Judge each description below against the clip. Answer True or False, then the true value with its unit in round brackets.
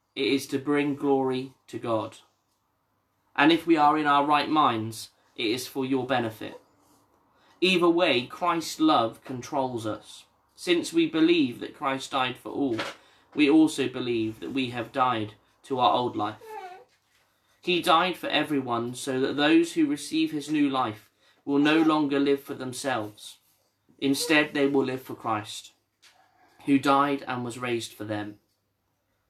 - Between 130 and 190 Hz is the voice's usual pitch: True (135 Hz)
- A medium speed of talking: True (155 wpm)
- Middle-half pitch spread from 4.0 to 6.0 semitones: True (5.2 semitones)